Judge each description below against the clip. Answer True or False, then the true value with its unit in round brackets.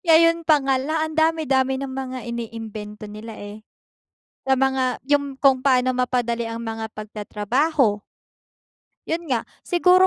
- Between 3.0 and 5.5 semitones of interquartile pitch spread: True (4.8 semitones)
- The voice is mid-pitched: False (260 Hz)